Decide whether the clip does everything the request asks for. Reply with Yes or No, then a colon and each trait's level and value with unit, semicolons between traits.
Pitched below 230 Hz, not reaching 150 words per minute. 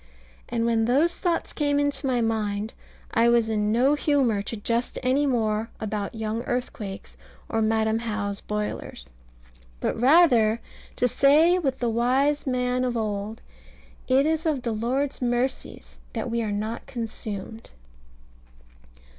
No: high, 235 Hz; average, 140 wpm